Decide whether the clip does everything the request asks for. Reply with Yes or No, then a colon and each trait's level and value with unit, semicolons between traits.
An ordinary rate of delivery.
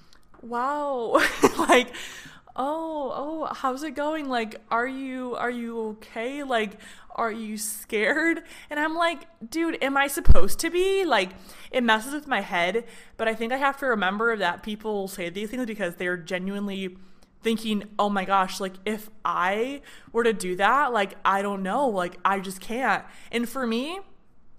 Yes: average, 170 wpm